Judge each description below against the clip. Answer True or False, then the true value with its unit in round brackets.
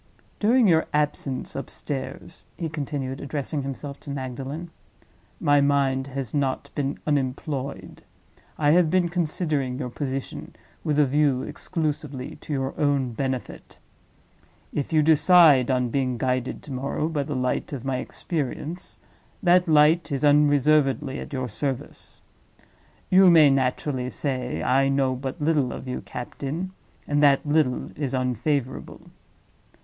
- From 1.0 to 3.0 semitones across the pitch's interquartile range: True (2.6 semitones)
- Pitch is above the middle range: False (140 Hz)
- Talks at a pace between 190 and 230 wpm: False (135 wpm)